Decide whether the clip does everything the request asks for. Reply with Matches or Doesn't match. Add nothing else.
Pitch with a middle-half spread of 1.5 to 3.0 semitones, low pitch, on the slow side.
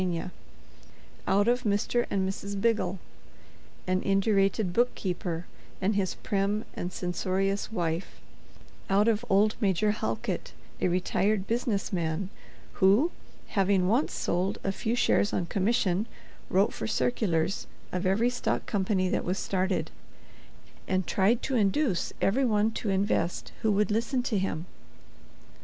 Doesn't match